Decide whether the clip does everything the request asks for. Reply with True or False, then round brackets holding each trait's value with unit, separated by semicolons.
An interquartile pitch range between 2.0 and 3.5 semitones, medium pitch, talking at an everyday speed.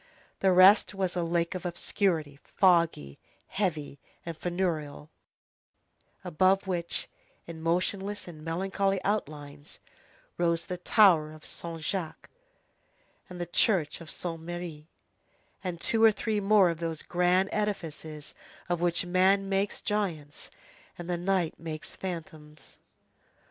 False (3.1 semitones; 175 Hz; 125 wpm)